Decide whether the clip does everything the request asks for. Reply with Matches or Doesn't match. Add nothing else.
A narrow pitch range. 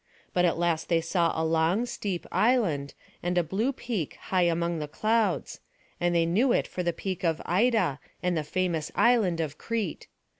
Doesn't match